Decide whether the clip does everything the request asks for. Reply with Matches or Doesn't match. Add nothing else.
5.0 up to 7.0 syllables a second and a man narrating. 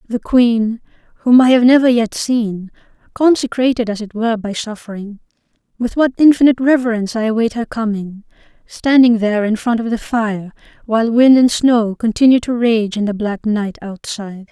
Doesn't match